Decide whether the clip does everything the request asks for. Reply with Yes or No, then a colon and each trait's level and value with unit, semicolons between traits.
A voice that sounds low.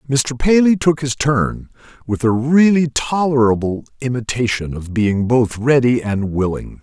Yes: low, 125 Hz